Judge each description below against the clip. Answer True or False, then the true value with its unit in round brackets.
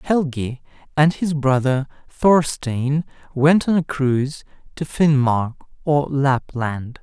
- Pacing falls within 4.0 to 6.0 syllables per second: False (3.5 syllables/s)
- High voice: False (140 Hz)